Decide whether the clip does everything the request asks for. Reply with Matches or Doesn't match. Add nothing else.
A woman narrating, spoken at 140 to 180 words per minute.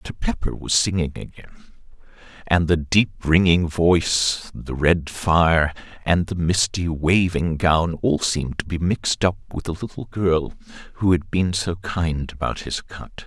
Doesn't match